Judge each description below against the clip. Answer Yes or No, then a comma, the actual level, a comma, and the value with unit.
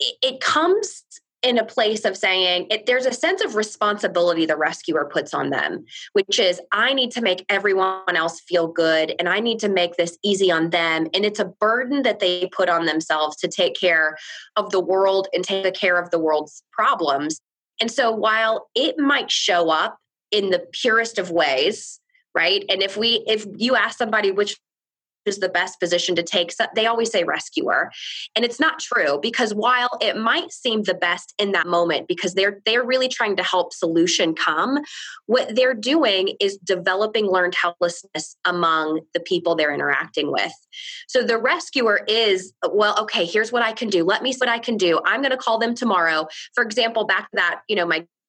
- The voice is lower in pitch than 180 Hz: No, high, 205 Hz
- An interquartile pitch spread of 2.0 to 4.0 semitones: No, wide, 5.5 semitones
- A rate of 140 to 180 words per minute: No, average, 200 wpm